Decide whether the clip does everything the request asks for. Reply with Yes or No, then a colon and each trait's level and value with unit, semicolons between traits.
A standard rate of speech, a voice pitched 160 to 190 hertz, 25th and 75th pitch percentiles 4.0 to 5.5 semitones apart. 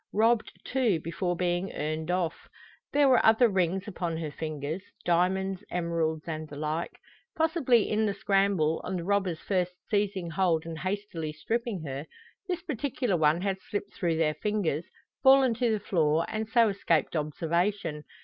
Yes: average, 160 wpm; medium, 185 Hz; average, 4.5 semitones